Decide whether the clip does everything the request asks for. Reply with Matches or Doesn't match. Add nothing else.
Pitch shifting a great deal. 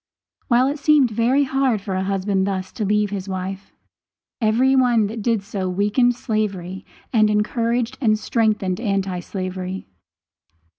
Doesn't match